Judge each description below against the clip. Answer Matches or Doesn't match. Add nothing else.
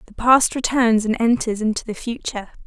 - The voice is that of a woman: Matches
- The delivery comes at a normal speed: Matches